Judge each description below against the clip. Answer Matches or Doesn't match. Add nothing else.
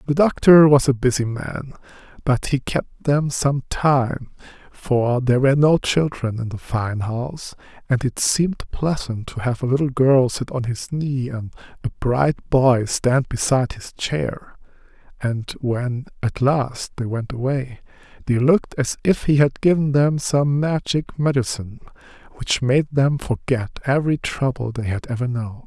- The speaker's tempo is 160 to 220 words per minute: Matches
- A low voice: Matches